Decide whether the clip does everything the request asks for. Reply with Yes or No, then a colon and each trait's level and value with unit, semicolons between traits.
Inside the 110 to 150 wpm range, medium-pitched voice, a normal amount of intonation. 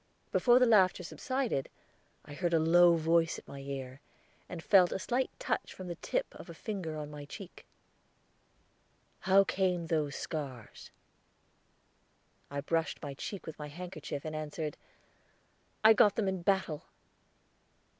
Yes: average, 145 wpm; medium, 170 Hz; average, 4.3 semitones